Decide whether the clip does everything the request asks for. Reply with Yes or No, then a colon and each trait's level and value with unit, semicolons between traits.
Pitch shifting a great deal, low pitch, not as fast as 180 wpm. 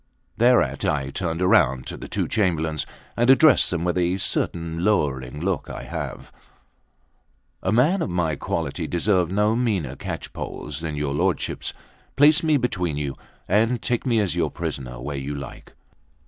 Yes: wide, 6.5 semitones; very low, 90 Hz; average, 160 wpm